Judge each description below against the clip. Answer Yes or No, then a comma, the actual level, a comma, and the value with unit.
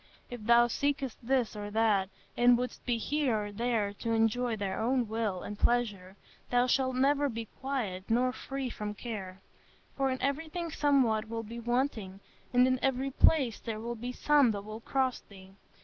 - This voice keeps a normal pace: Yes, average, 180 wpm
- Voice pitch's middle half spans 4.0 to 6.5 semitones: No, average, 3.4 semitones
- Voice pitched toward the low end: No, high, 240 Hz